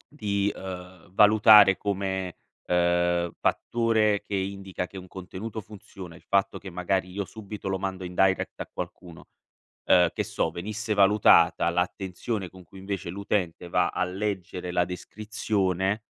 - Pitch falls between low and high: No, very low, 95 Hz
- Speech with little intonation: Yes, narrow, 2.1 semitones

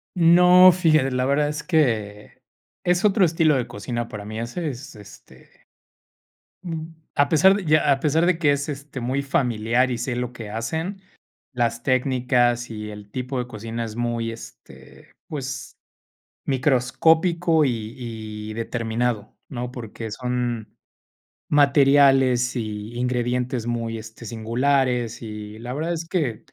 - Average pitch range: Yes, average, 4.2 semitones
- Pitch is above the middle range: No, low, 125 Hz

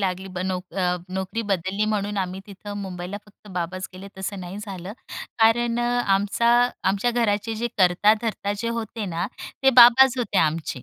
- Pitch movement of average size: Yes, average, 3.4 semitones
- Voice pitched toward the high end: Yes, high, 200 Hz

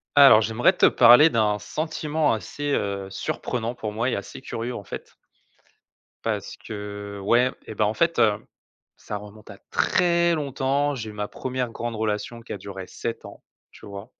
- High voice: No, low, 115 Hz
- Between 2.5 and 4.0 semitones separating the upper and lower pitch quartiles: No, average, 4.5 semitones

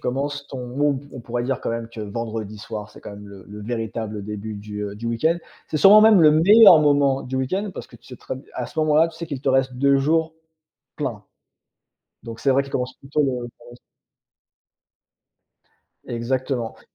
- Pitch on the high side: No, low, 130 Hz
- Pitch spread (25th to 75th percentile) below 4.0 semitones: No, average, 4.3 semitones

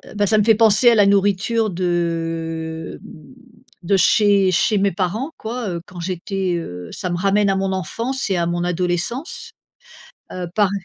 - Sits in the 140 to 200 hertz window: Yes, high, 190 Hz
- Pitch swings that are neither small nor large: Yes, average, 3.2 semitones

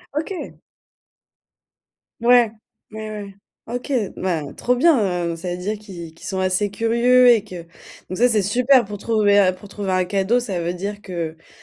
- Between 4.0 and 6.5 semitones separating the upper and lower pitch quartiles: Yes, average, 4.3 semitones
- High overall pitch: Yes, high, 205 Hz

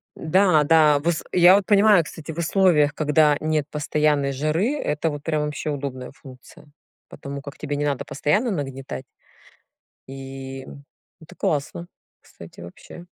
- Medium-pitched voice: Yes, medium, 150 Hz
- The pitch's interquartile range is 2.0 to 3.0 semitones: Yes, average, 2.7 semitones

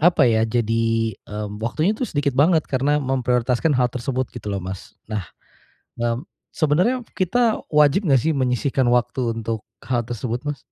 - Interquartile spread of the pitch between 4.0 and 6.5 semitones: Yes, average, 4.3 semitones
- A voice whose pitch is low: Yes, low, 125 Hz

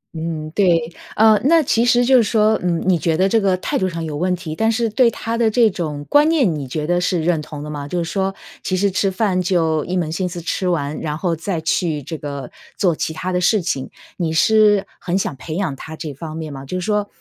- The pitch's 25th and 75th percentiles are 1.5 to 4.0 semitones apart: No, average, 4.5 semitones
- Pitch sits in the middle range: Yes, medium, 180 Hz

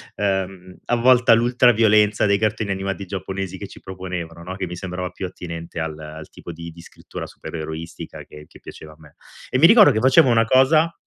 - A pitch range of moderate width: Yes, average, 5.0 semitones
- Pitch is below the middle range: Yes, very low, 95 Hz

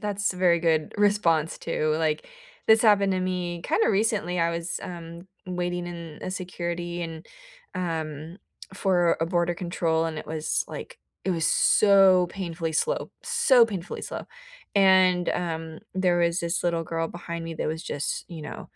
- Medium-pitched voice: Yes, medium, 175 Hz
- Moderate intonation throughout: No, narrow, 2.1 semitones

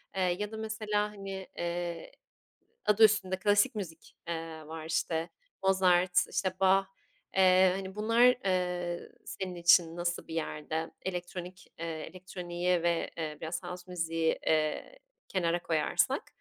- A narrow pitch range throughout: Yes, narrow, 2.1 semitones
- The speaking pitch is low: No, medium, 180 Hz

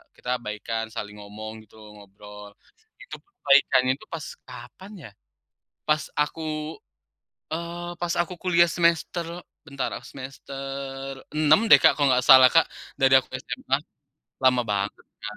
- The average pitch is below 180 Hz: Yes, low, 135 Hz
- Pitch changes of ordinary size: No, wide, 6.5 semitones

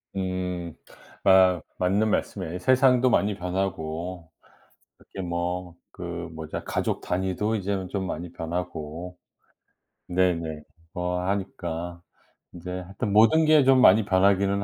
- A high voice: No, very low, 90 Hz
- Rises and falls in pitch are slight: Yes, narrow, 2.3 semitones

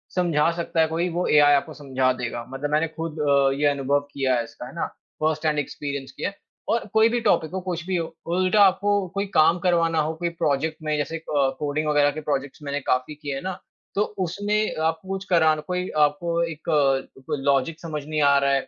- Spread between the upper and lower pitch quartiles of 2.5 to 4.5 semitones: Yes, average, 3.3 semitones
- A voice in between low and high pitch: Yes, medium, 155 Hz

